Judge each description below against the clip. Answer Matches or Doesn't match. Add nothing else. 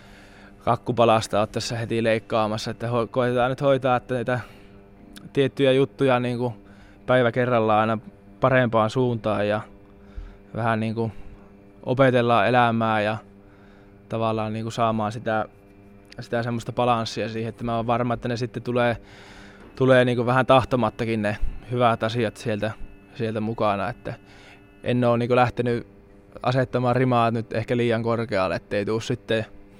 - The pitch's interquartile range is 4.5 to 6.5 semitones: Doesn't match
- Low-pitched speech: Matches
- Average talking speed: Matches